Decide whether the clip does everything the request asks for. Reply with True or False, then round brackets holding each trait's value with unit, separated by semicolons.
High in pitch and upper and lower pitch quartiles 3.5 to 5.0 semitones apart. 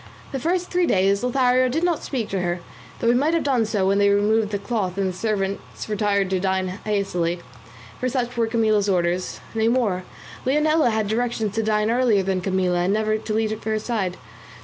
True (215 Hz; 3.9 semitones)